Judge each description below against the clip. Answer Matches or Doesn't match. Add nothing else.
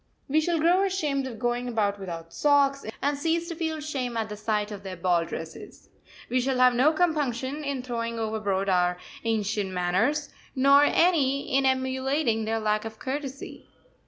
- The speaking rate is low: Doesn't match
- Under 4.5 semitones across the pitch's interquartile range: Doesn't match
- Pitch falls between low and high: Doesn't match